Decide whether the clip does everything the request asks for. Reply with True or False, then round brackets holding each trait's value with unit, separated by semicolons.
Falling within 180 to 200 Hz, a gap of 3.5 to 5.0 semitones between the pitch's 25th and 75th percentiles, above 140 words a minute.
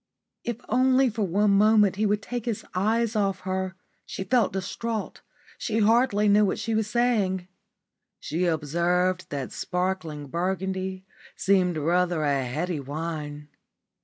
False (190 Hz; 3.8 semitones; 135 wpm)